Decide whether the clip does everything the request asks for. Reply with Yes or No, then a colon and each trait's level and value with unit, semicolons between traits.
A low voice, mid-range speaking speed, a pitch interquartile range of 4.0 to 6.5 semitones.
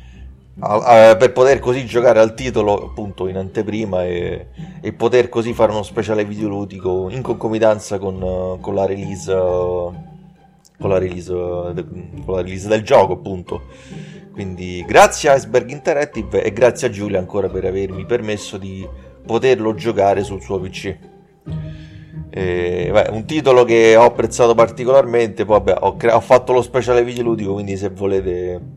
Yes: low, 105 Hz; average, 150 wpm; average, 4.5 semitones